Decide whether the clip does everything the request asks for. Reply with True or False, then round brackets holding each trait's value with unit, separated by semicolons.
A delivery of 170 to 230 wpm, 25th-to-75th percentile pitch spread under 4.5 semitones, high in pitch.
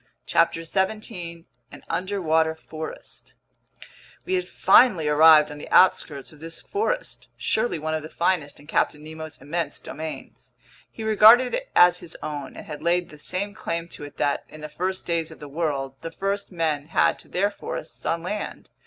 False (180 wpm; 3.7 semitones; 165 Hz)